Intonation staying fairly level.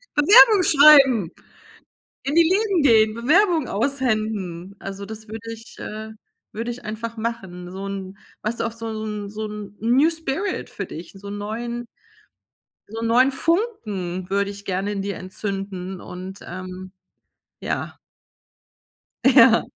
No: average, 4.5 semitones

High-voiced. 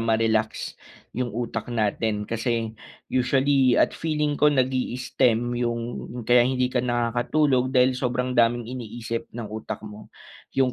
No: low, 120 Hz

